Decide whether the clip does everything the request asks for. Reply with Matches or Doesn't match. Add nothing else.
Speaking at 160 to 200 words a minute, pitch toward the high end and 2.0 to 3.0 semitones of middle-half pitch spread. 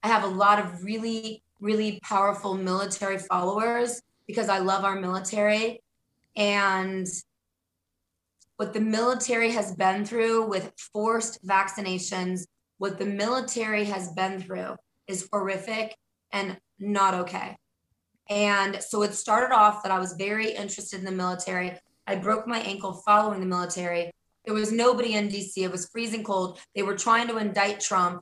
Doesn't match